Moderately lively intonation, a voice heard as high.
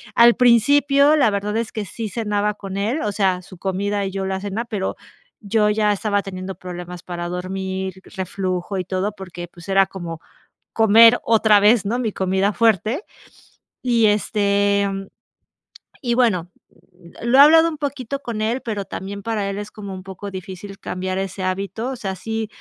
Yes: average, 3.0 semitones; high, 200 Hz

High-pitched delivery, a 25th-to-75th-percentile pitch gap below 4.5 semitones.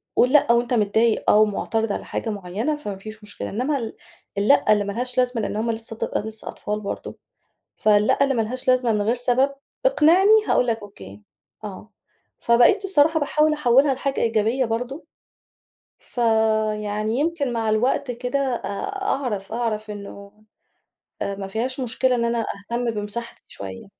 Yes: high, 230 Hz; average, 3.5 semitones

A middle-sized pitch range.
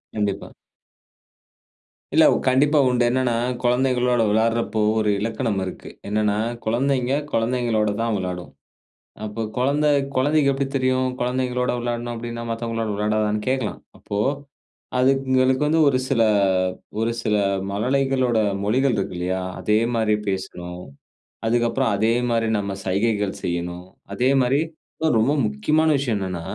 Yes: average, 3.5 semitones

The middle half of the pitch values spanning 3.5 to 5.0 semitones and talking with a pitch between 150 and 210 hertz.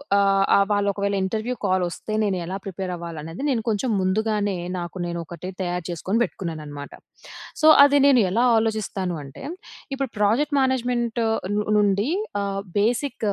Yes: average, 3.8 semitones; high, 200 Hz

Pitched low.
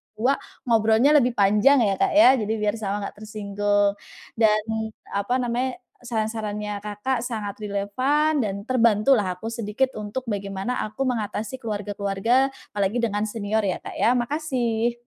No: high, 215 Hz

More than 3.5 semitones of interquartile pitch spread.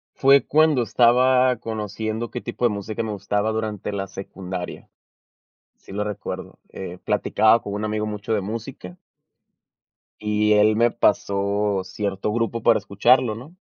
No: narrow, 2.5 semitones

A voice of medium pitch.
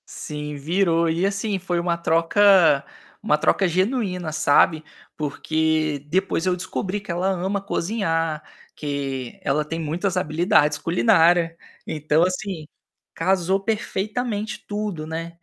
Yes: medium, 170 Hz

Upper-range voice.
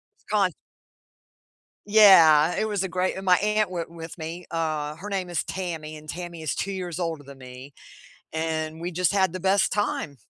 No: medium, 170 Hz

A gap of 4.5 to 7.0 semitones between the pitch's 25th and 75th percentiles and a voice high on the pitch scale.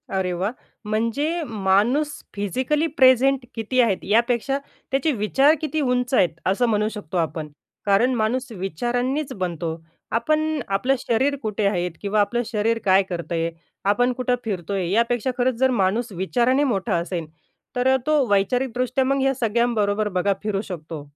Yes: average, 4.8 semitones; high, 230 Hz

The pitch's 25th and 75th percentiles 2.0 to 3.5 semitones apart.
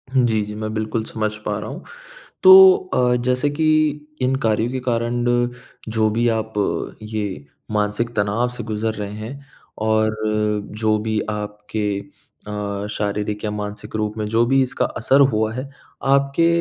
Yes: average, 2.9 semitones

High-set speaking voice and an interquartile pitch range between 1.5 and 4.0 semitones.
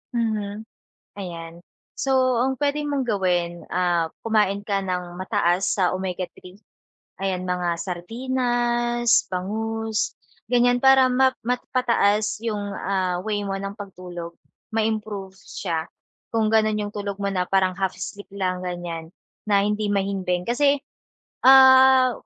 No: high, 200 Hz; average, 4.6 semitones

